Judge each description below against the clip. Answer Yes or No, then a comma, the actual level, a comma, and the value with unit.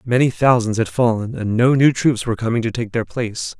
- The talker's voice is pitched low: Yes, low, 120 Hz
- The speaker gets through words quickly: Yes, fast, 235 wpm